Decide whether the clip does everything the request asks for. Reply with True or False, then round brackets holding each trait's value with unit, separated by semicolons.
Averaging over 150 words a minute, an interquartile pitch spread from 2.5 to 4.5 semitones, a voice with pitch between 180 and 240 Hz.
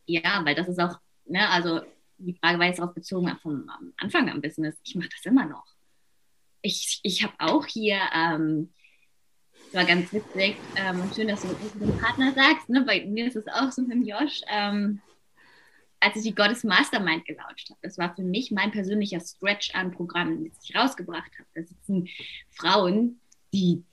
True (190 wpm; 3.8 semitones; 190 Hz)